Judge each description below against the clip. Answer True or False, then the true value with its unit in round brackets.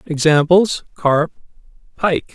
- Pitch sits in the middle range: True (160 Hz)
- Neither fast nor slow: False (75 wpm)